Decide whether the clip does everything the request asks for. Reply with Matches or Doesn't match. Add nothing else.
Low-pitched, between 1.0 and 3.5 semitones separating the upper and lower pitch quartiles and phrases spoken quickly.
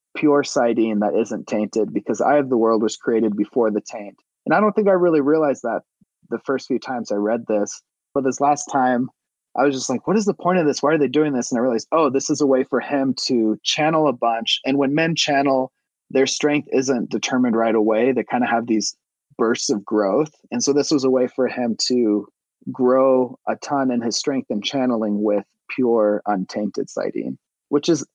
Doesn't match